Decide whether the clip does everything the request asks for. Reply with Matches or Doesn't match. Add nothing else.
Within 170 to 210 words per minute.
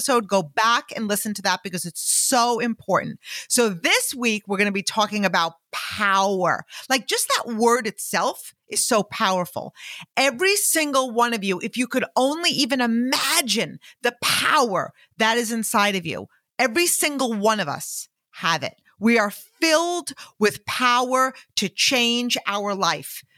Doesn't match